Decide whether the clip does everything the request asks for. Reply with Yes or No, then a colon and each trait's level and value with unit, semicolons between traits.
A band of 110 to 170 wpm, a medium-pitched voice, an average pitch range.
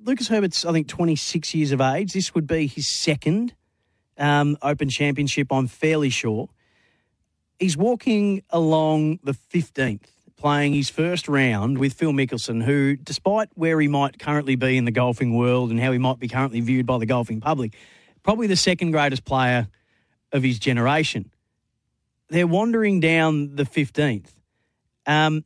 Yes: average, 160 wpm; medium, 145 Hz; average, 4.3 semitones